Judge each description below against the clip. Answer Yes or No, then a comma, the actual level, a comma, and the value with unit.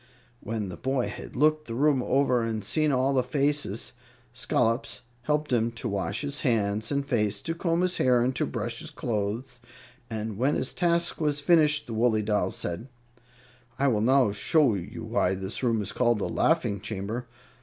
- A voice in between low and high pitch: No, low, 125 Hz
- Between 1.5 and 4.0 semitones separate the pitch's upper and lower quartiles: No, average, 4.6 semitones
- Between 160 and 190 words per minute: Yes, average, 185 wpm